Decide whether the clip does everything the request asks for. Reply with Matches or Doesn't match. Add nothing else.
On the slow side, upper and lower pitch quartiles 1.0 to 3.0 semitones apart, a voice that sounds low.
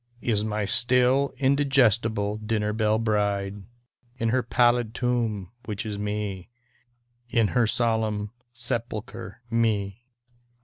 Matches